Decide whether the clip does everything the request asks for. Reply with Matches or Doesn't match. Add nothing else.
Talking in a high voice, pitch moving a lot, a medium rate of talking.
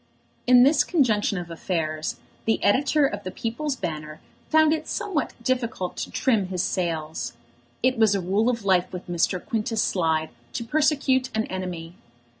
Matches